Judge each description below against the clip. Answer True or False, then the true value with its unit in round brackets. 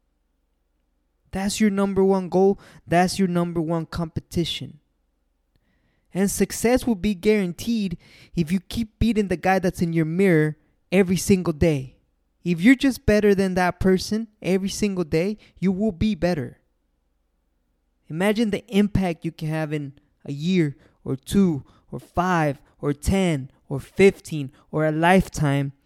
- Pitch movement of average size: False (5.9 semitones)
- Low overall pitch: False (175 Hz)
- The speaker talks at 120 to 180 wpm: True (145 wpm)